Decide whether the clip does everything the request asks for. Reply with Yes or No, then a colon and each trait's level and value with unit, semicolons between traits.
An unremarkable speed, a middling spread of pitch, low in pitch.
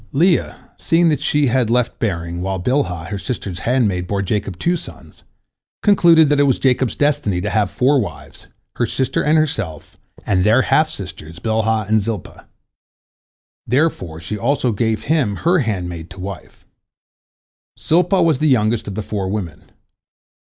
No: average, 160 wpm; wide, 6.9 semitones; low, 110 Hz